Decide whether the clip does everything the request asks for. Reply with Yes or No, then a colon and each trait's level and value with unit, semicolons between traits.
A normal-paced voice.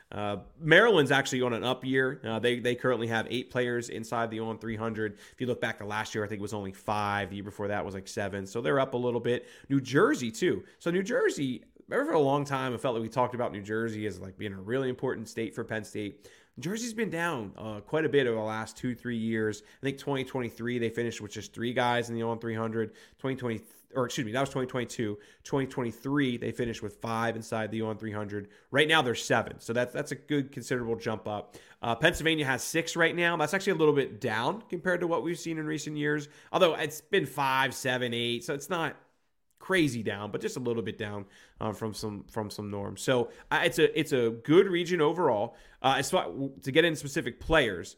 No: fast, 235 wpm